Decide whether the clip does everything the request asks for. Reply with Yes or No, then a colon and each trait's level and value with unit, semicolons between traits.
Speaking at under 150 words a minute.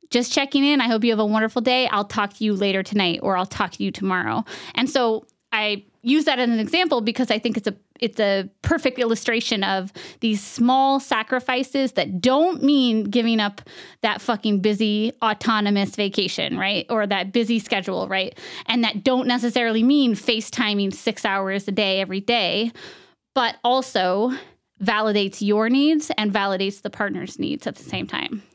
No: average, 180 wpm